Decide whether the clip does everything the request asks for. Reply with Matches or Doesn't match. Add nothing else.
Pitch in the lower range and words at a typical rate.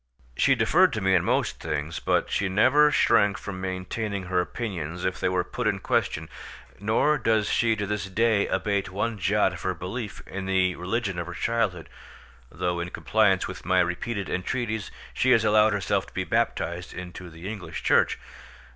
Matches